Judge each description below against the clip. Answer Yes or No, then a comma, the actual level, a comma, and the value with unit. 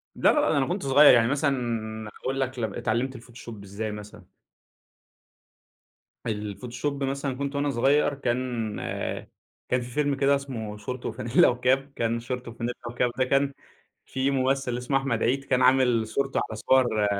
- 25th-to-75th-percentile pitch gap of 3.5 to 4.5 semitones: No, average, 3.0 semitones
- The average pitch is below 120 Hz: No, low, 125 Hz